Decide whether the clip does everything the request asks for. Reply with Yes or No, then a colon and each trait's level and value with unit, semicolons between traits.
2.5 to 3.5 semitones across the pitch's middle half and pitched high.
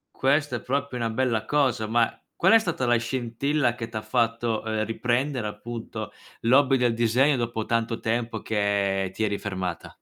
No: average, 2.8 semitones; low, 115 Hz